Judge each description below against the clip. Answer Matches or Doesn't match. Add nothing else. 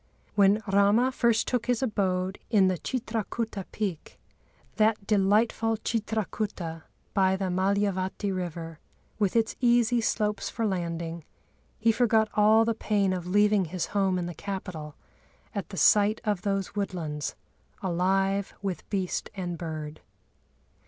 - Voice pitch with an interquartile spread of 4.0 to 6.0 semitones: Doesn't match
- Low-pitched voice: Doesn't match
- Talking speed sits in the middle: Doesn't match